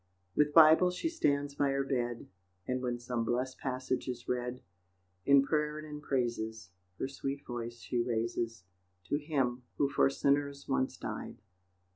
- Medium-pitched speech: No, low, 130 Hz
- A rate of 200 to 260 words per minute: No, average, 155 wpm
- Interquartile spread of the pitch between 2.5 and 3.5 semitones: Yes, average, 2.9 semitones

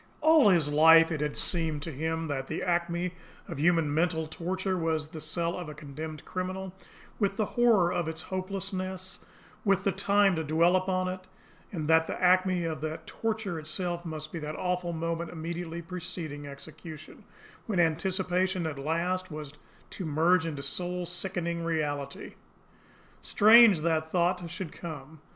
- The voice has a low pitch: No, medium, 170 Hz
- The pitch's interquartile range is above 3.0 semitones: No, average, 2.7 semitones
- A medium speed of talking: Yes, average, 160 wpm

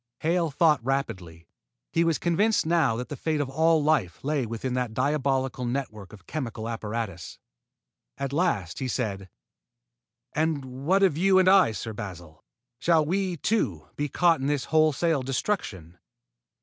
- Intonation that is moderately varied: No, wide, 6.3 semitones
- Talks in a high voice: No, low, 135 Hz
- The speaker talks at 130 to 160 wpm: Yes, average, 150 wpm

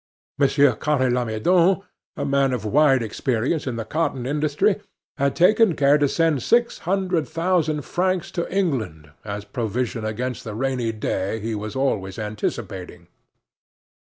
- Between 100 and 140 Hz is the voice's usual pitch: Yes, low, 135 Hz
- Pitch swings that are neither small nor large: No, wide, 6.5 semitones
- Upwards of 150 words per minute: No, average, 140 wpm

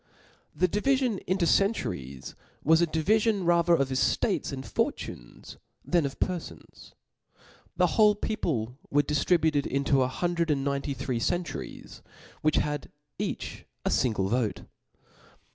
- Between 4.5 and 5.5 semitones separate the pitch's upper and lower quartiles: Yes, average, 5.1 semitones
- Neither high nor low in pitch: Yes, medium, 155 Hz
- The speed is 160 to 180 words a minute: No, average, 145 wpm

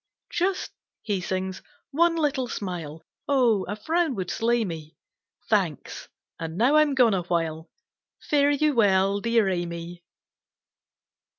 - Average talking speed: No, slow, 120 wpm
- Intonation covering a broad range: Yes, wide, 7.8 semitones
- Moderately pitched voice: No, high, 210 Hz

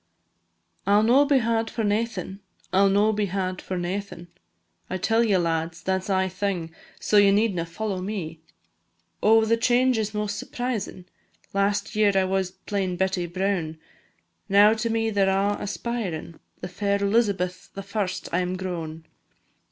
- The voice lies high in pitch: Yes, high, 195 Hz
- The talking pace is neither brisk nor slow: Yes, average, 165 wpm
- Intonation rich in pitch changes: No, average, 2.7 semitones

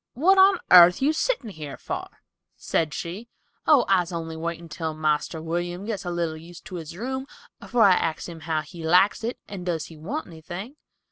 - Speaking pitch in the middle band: Yes, medium, 175 Hz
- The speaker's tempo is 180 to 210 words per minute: Yes, average, 195 wpm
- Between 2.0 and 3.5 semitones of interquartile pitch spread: No, average, 4.8 semitones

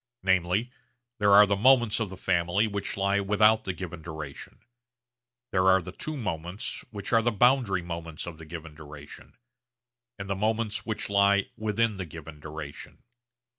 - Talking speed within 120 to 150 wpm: No, average, 160 wpm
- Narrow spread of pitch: No, average, 4.1 semitones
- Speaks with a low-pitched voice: Yes, very low, 95 Hz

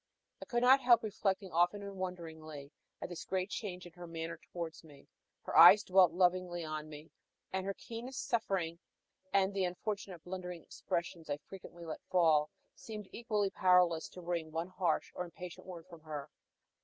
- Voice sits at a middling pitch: Yes, medium, 180 Hz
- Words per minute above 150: Yes, average, 170 wpm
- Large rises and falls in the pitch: No, average, 2.9 semitones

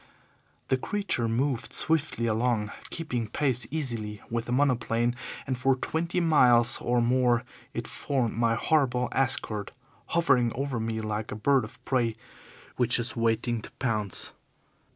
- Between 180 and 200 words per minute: No, average, 140 wpm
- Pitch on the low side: Yes, low, 120 Hz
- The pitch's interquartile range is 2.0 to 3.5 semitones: Yes, average, 2.9 semitones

